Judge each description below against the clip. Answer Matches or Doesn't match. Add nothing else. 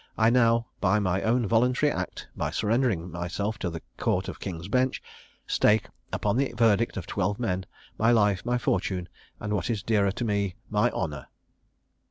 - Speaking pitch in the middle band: Doesn't match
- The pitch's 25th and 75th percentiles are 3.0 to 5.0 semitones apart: Matches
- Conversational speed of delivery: Matches